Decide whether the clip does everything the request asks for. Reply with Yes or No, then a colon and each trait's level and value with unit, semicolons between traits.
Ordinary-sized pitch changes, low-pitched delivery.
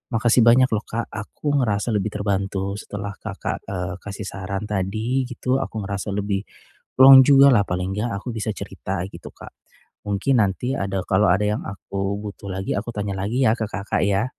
Yes: average, 3.0 semitones; low, 105 Hz